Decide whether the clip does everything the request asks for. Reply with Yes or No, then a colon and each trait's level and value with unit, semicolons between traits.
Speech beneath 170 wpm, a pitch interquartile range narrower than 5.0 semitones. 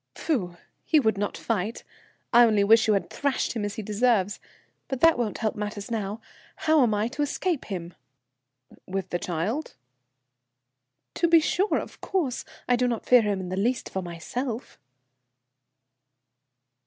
Yes: average, 160 wpm; average, 4.2 semitones